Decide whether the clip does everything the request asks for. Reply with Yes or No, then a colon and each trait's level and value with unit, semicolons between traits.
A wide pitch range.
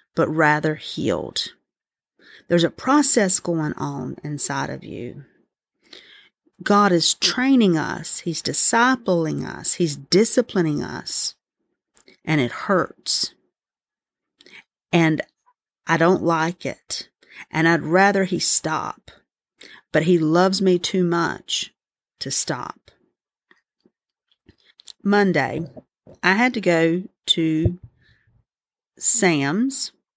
No: average, 4.1 semitones